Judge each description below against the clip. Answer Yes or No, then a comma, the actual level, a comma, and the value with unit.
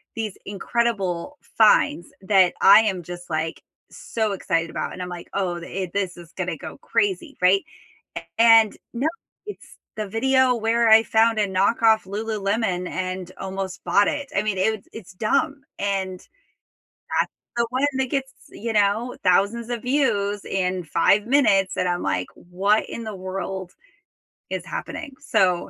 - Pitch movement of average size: Yes, average, 3.7 semitones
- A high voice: Yes, high, 200 Hz